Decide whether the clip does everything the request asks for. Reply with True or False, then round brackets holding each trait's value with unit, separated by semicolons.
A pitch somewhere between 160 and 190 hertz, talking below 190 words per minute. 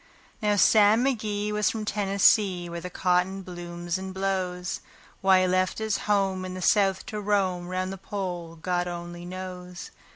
True (185 Hz; 165 wpm)